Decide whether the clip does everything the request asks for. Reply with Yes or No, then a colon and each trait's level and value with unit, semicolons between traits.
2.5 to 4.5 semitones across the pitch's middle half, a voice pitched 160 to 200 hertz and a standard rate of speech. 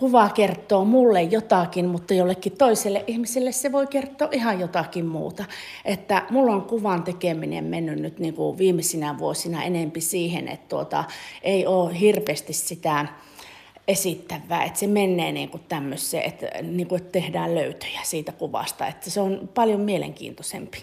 Yes: average, 3.5 semitones; medium, 185 Hz; average, 145 wpm